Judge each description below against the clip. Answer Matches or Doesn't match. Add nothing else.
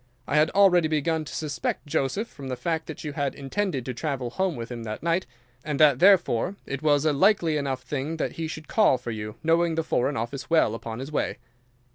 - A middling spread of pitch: Matches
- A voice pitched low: Doesn't match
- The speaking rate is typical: Doesn't match